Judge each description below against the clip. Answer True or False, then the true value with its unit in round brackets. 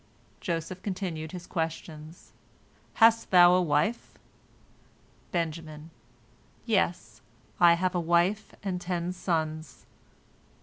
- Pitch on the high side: False (175 Hz)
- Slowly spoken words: True (95 wpm)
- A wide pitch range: False (2.4 semitones)